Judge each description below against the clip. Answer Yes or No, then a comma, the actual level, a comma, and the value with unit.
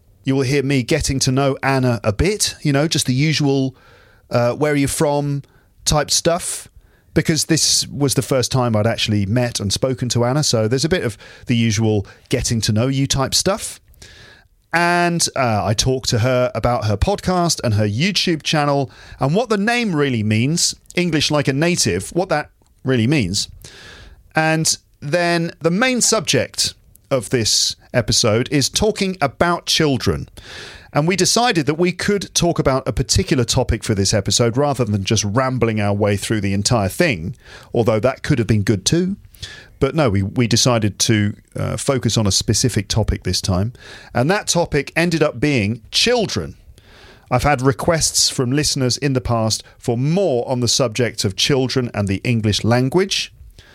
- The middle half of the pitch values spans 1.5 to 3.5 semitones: No, wide, 5.5 semitones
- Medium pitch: No, low, 125 Hz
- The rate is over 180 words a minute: No, average, 175 wpm